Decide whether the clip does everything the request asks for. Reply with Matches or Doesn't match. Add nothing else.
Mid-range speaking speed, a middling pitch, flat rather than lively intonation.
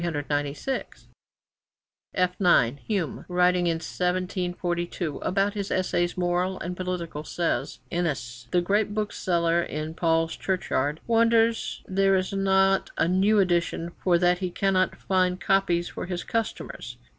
Doesn't match